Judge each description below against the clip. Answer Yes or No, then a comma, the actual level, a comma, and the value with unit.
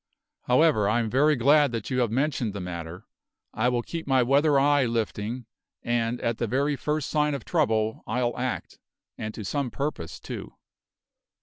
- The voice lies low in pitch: Yes, low, 125 Hz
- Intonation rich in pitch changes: No, average, 4.3 semitones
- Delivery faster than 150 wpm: Yes, average, 175 wpm